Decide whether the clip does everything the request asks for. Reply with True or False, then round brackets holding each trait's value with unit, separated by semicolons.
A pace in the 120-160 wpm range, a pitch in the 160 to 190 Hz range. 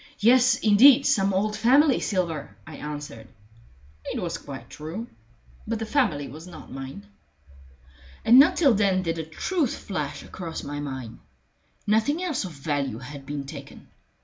True (150 wpm; 185 Hz)